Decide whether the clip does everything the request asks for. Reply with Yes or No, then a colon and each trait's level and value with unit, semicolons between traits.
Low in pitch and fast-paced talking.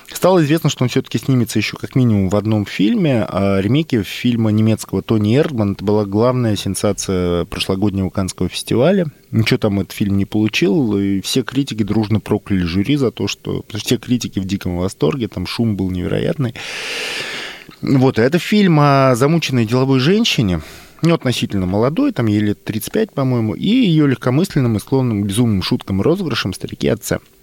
Yes: low, 115 Hz; fast, 170 wpm